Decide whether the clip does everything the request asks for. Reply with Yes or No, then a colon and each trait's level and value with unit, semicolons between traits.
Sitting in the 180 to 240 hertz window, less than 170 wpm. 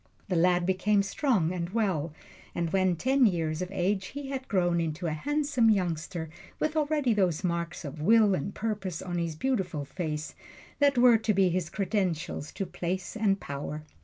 No: medium, 185 Hz; average, 175 wpm